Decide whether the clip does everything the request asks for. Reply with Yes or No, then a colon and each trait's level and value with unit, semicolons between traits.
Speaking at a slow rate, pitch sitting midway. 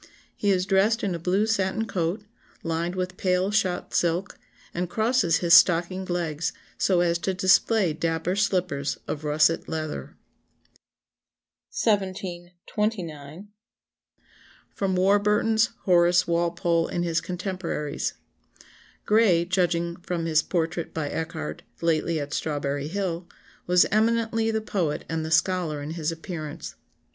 Yes: slow, 125 wpm; medium, 175 Hz